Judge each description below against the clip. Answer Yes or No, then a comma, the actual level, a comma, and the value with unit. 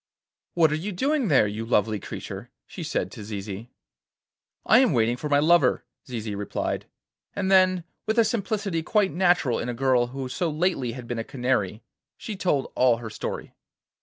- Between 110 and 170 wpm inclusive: No, average, 180 wpm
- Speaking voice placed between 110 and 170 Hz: Yes, low, 135 Hz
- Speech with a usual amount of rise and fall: No, wide, 8.1 semitones